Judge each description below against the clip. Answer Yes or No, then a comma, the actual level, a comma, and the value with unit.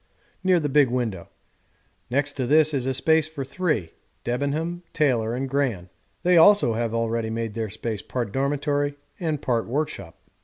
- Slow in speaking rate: No, average, 160 wpm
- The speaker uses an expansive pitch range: No, average, 4.7 semitones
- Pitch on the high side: No, low, 135 Hz